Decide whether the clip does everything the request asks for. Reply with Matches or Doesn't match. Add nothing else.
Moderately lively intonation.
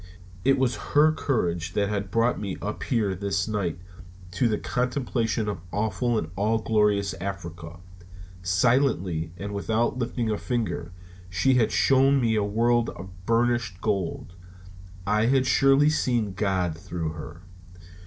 Matches